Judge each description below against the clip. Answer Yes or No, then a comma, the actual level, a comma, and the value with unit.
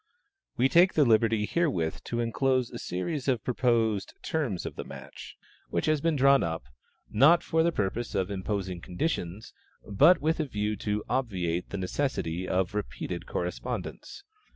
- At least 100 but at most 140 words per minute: No, average, 155 wpm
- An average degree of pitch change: No, wide, 6.7 semitones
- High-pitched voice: No, low, 115 Hz